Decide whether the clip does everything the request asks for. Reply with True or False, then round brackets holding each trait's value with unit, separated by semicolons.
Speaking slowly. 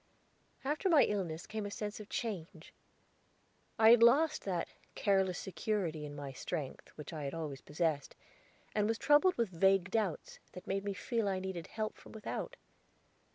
False (165 wpm)